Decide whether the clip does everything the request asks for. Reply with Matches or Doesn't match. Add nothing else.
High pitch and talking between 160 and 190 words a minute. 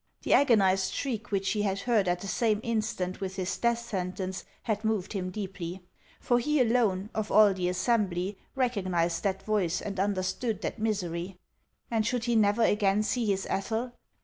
Matches